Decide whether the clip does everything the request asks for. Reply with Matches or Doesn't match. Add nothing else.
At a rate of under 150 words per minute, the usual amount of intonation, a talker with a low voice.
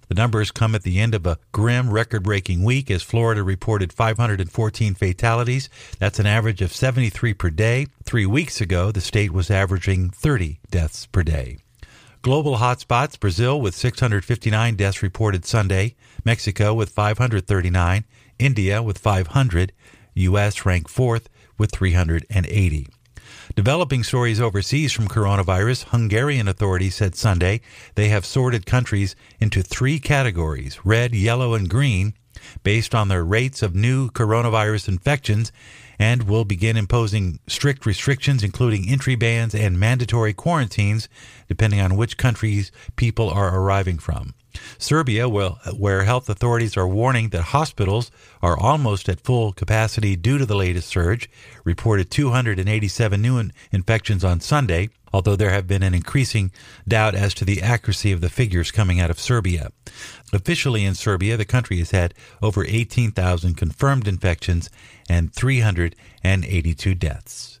Matches